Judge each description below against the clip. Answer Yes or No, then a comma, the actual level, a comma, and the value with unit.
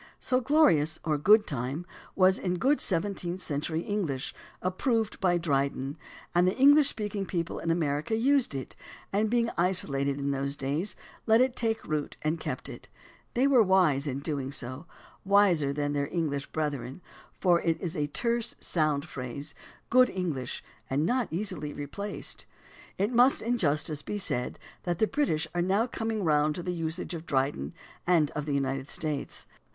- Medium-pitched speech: Yes, medium, 170 Hz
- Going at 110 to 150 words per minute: No, average, 170 wpm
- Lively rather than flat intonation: Yes, wide, 6.2 semitones